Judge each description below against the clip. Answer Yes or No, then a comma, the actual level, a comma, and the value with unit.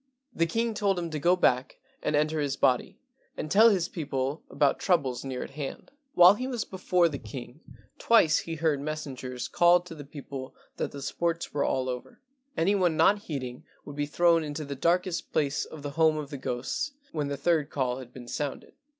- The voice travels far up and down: No, average, 4.0 semitones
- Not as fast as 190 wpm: No, average, 200 wpm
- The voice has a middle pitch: Yes, medium, 150 Hz